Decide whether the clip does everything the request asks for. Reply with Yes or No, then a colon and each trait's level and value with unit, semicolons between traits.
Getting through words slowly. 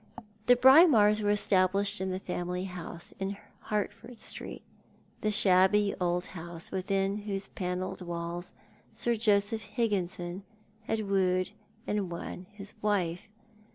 Yes: slow, 125 wpm